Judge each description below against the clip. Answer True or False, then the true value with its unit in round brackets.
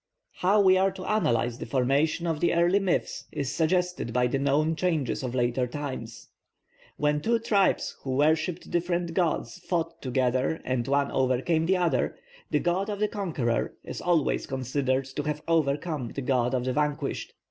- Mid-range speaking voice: True (150 Hz)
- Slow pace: False (170 wpm)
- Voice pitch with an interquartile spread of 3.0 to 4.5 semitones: False (5.0 semitones)